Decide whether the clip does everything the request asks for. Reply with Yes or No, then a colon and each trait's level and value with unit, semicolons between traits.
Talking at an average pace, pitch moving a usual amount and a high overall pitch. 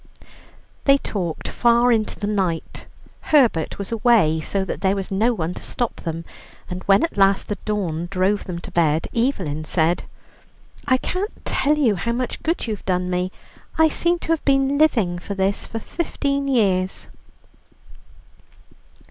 No: average, 160 wpm; wide, 5.8 semitones; high, 205 Hz